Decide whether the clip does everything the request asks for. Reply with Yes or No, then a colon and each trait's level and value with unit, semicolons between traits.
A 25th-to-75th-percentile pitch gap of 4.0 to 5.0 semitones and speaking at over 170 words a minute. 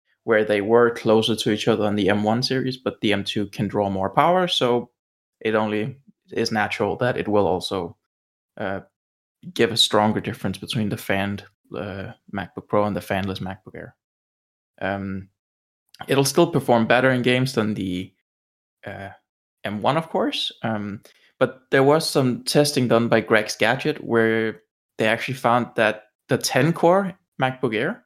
No: average, 4.4 semitones; average, 165 wpm